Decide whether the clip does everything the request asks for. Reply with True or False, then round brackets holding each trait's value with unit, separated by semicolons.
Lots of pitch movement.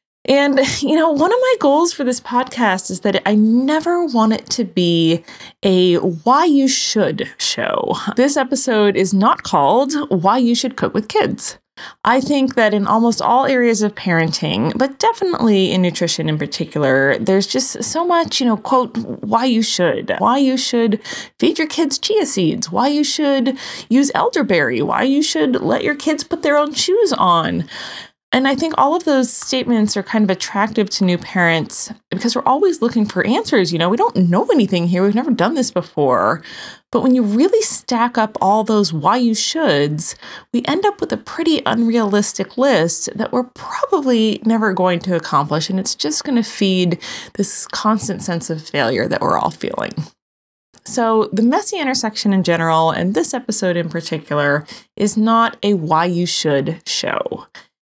True (6.4 semitones)